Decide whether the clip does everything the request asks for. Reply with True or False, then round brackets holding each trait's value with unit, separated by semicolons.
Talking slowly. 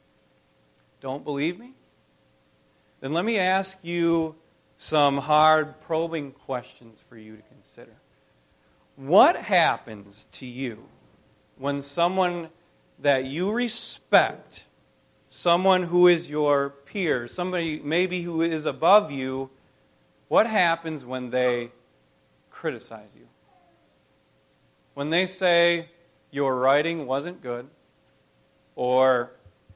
True (100 wpm)